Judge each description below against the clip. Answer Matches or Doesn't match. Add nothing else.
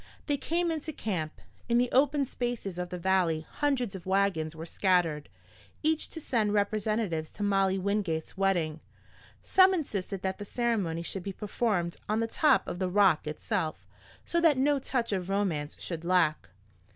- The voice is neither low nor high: Doesn't match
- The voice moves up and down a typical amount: Doesn't match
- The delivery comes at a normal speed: Matches